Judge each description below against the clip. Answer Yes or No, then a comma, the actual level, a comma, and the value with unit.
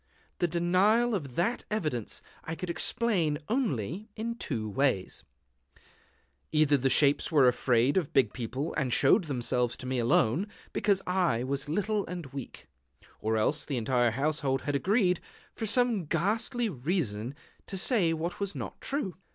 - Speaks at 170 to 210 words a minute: No, average, 150 wpm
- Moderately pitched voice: Yes, medium, 155 Hz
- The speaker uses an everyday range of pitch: No, wide, 7.2 semitones